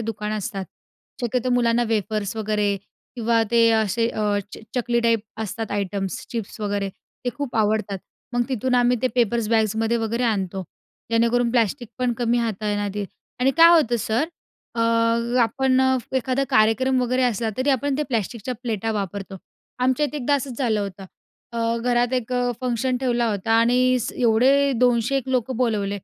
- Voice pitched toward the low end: No, high, 230 Hz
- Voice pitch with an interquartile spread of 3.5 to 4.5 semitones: No, average, 2.7 semitones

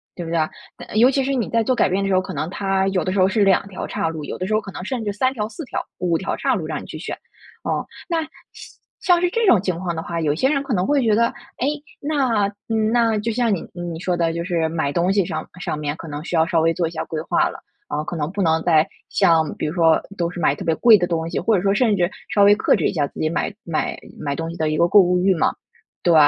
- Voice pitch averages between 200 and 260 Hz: No, medium, 185 Hz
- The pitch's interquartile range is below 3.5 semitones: No, average, 4.8 semitones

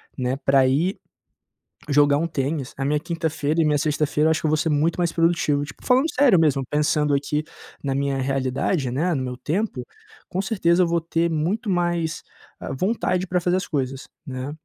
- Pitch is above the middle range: No, medium, 155 Hz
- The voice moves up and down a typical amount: Yes, average, 3.7 semitones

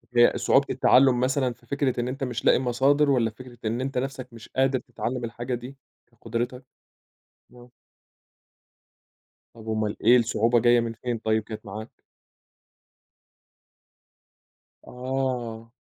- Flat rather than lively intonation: Yes, narrow, 2.1 semitones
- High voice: No, low, 120 Hz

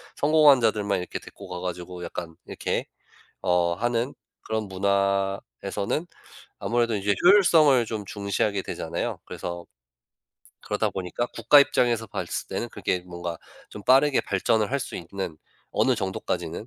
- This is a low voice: Yes, low, 100 Hz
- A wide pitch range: No, average, 5.0 semitones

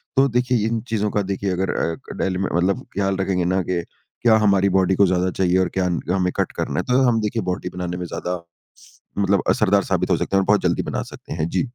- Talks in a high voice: No, very low, 95 Hz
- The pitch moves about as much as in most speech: No, narrow, 2.2 semitones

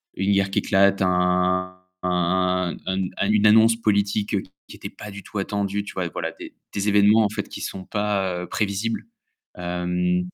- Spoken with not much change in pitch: Yes, narrow, 2.1 semitones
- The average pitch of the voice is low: Yes, very low, 95 Hz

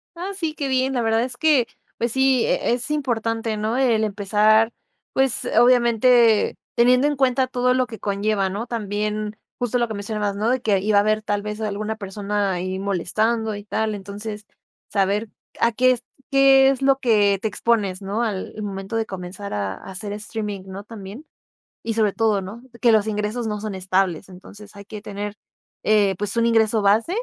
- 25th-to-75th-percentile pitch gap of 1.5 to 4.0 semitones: Yes, average, 2.8 semitones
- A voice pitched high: Yes, high, 215 Hz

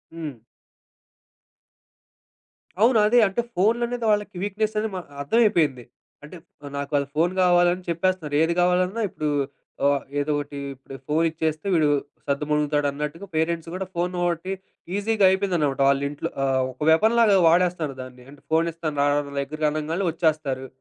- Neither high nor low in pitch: Yes, medium, 165 Hz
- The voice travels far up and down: No, average, 4.2 semitones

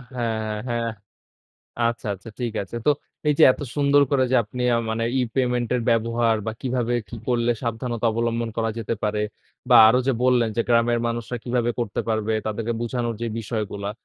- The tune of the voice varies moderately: No, narrow, 1.4 semitones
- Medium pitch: No, low, 115 Hz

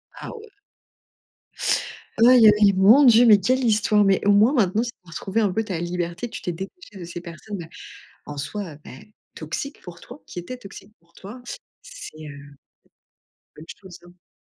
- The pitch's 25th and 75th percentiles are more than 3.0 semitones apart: Yes, average, 4.7 semitones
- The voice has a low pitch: No, high, 200 Hz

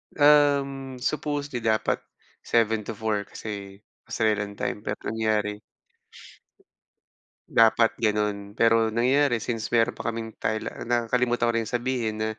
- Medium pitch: No, low, 115 Hz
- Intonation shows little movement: Yes, narrow, 2.2 semitones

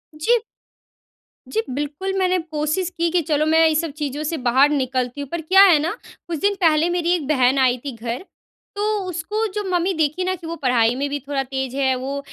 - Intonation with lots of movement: No, average, 4.4 semitones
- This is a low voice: No, very high, 305 Hz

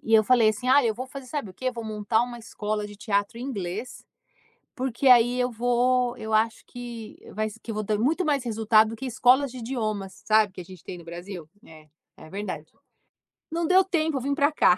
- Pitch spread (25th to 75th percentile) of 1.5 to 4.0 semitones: Yes, average, 3.4 semitones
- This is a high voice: Yes, high, 230 Hz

